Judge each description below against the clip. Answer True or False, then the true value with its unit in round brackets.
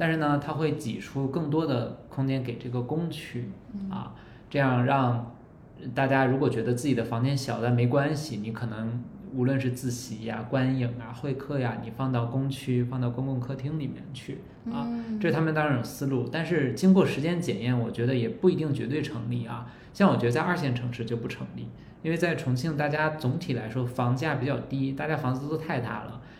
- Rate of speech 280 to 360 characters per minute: True (300 characters per minute)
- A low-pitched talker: True (130 Hz)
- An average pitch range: True (3.8 semitones)